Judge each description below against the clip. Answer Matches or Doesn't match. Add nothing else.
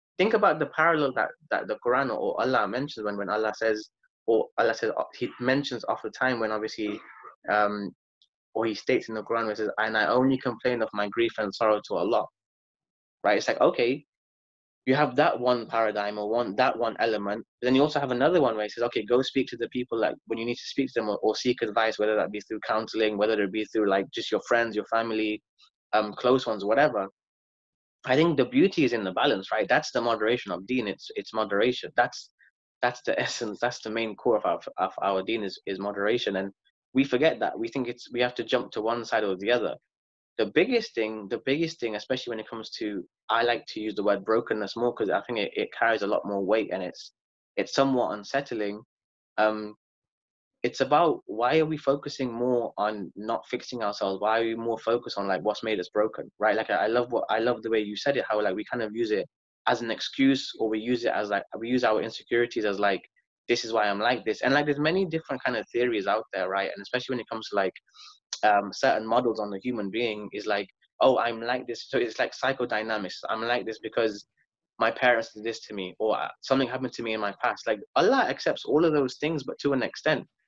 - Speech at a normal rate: Doesn't match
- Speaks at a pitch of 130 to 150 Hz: Doesn't match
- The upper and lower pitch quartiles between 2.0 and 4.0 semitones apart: Matches